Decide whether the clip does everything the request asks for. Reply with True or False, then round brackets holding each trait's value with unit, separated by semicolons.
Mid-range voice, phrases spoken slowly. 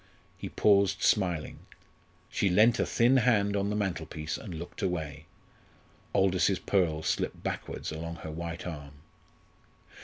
False (90 Hz; 130 wpm)